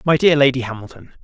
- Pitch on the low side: Yes, low, 130 Hz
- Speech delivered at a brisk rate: No, average, 195 wpm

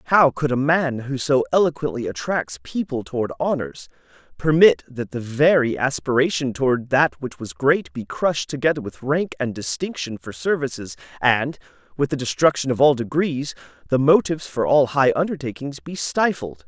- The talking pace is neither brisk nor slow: Yes, average, 160 wpm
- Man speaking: Yes, male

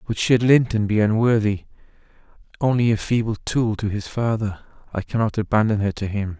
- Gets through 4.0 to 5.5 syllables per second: Yes, 5.4 syllables/s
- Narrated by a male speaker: Yes, male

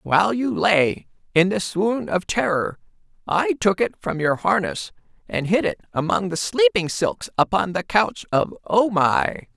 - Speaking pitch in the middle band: Yes, medium, 170 Hz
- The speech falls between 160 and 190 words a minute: Yes, average, 170 wpm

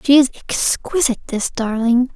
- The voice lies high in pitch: Yes, very high, 250 Hz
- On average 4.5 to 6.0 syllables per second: Yes, 5.2 syllables/s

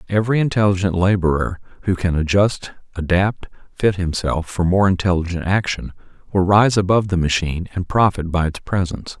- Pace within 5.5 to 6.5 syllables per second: Yes, 5.6 syllables/s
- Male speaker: Yes, male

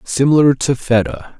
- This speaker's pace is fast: No, slow, 130 wpm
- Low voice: Yes, low, 125 Hz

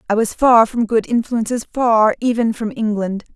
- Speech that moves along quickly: No, average, 160 wpm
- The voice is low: No, high, 225 Hz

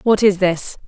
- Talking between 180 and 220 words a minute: Yes, fast, 205 wpm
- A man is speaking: No, female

